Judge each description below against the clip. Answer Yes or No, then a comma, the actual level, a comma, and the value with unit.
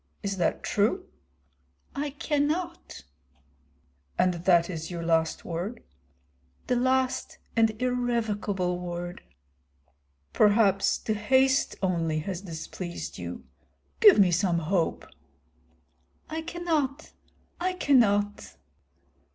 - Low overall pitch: No, high, 205 Hz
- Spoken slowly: Yes, slow, 95 wpm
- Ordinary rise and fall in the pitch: No, wide, 6.9 semitones